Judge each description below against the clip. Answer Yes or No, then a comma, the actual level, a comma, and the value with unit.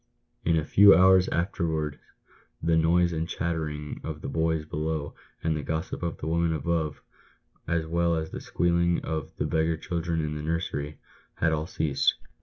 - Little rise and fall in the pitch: Yes, narrow, 1.6 semitones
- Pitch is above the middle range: No, very low, 80 Hz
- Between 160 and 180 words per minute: Yes, average, 170 wpm